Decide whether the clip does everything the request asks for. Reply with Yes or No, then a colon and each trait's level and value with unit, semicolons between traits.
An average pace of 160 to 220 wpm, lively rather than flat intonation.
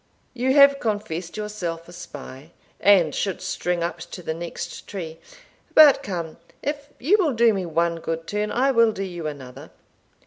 Yes: average, 170 wpm; wide, 5.7 semitones